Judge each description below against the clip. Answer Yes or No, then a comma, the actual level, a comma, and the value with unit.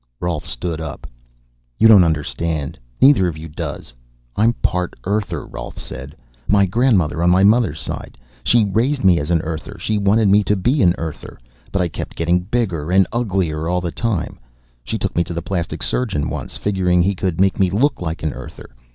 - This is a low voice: Yes, very low, 90 Hz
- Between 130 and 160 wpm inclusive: No, average, 195 wpm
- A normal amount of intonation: Yes, average, 4.1 semitones